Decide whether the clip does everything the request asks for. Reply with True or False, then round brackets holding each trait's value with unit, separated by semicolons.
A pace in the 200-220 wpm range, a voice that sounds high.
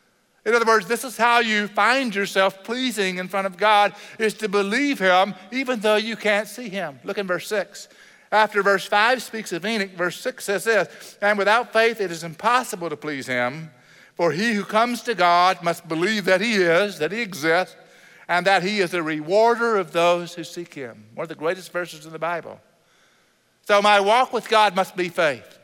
True (205 wpm; 200 Hz)